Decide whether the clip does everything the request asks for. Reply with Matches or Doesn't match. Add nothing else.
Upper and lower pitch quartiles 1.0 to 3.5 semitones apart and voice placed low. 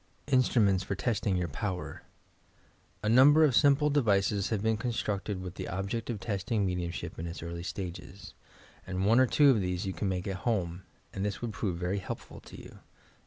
Doesn't match